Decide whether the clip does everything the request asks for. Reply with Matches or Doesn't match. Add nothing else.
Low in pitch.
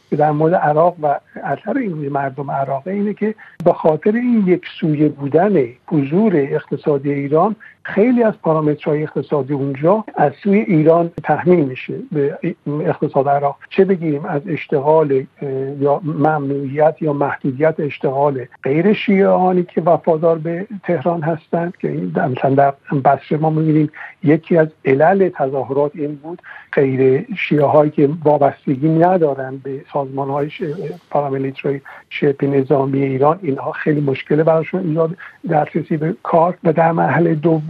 Doesn't match